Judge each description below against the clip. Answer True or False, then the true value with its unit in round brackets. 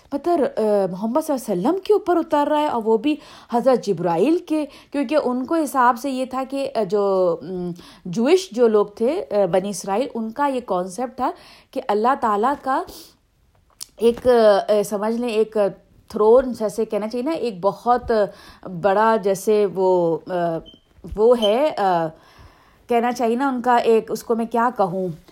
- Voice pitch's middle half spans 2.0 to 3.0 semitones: False (4.6 semitones)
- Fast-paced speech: False (160 wpm)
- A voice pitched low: False (230 Hz)